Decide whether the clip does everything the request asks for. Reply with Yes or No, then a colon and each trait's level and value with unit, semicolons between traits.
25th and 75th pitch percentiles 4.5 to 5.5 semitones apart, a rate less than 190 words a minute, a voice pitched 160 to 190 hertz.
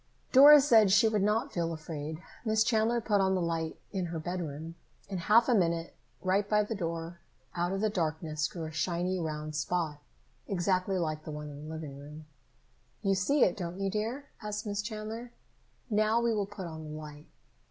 No: average, 5.0 semitones; average, 195 wpm; medium, 185 Hz